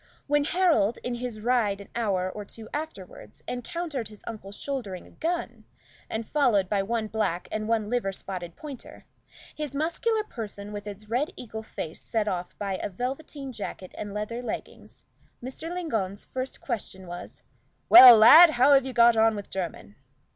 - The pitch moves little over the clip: No, average, 4.9 semitones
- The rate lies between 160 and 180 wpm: Yes, average, 170 wpm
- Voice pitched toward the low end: No, high, 225 Hz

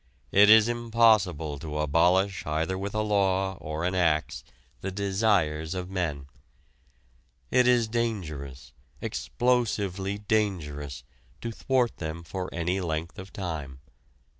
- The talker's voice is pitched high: No, very low, 95 Hz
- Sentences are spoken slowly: Yes, slow, 120 wpm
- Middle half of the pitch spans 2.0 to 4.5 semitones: No, average, 5.0 semitones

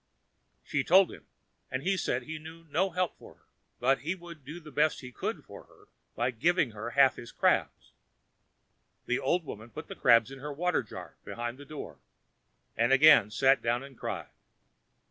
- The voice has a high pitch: No, medium, 140 Hz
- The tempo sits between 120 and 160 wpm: No, average, 185 wpm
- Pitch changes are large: No, average, 4.8 semitones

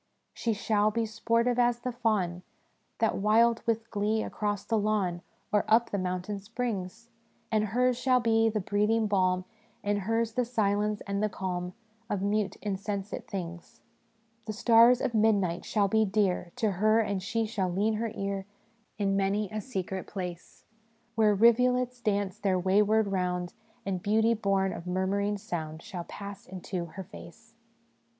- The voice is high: Yes, high, 210 Hz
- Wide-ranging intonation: No, average, 2.8 semitones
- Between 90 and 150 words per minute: No, average, 165 wpm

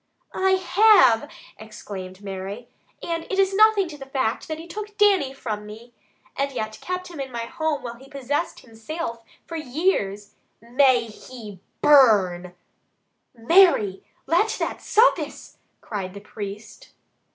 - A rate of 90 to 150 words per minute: Yes, average, 145 wpm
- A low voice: No, very high, 255 Hz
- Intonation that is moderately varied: No, wide, 7.8 semitones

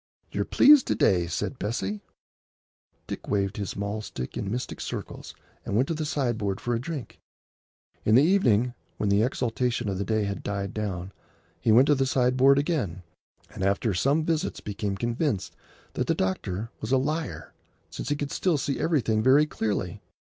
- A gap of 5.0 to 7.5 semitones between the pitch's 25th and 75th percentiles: Yes, wide, 5.5 semitones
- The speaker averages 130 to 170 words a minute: No, average, 180 wpm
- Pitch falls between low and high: No, low, 115 Hz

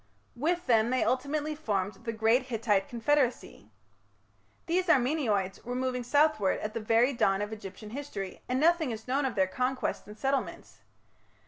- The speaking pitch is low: No, high, 245 Hz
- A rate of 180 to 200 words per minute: No, average, 155 wpm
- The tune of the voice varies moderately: Yes, average, 4.7 semitones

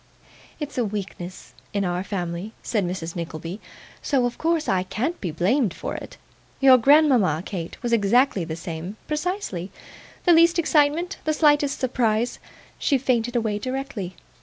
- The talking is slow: No, average, 150 wpm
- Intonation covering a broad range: Yes, wide, 7.6 semitones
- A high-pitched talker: Yes, high, 230 Hz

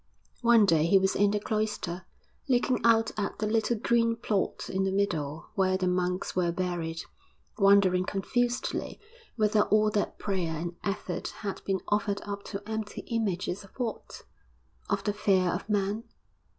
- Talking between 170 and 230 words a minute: No, average, 160 wpm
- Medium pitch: No, high, 200 Hz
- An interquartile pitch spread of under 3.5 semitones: Yes, average, 2.7 semitones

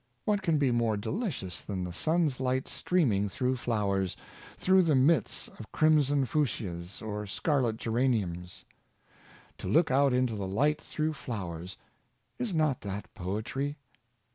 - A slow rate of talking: No, average, 150 wpm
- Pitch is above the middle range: No, low, 125 Hz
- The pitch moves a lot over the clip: Yes, wide, 6.9 semitones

